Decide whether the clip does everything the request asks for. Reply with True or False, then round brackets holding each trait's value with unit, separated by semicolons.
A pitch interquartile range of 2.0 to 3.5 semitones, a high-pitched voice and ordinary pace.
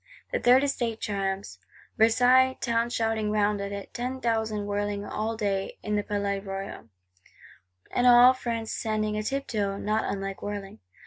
True (2.6 semitones; 215 Hz; 145 wpm)